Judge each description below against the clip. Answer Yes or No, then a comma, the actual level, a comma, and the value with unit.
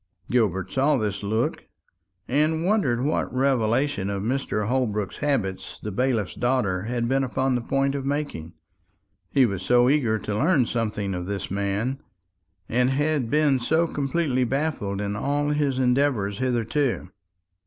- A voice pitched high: No, low, 125 Hz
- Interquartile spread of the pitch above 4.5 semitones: Yes, average, 5.0 semitones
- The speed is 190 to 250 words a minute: No, average, 145 wpm